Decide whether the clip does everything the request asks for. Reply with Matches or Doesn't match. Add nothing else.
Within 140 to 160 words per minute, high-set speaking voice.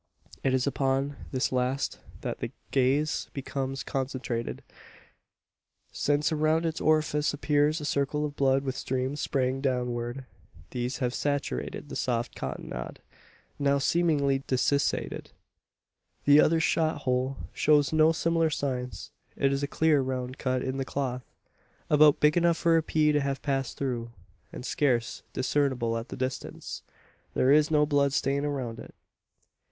Doesn't match